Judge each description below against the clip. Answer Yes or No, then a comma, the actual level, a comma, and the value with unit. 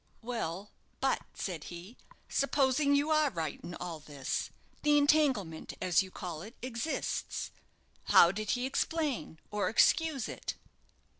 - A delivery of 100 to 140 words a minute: Yes, slow, 135 wpm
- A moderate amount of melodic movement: No, wide, 8.4 semitones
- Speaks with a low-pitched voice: No, high, 230 Hz